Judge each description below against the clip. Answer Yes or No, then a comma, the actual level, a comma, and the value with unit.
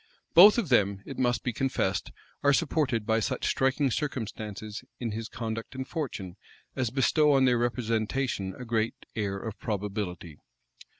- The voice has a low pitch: Yes, low, 115 Hz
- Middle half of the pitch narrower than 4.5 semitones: Yes, average, 4.0 semitones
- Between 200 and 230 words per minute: No, average, 155 wpm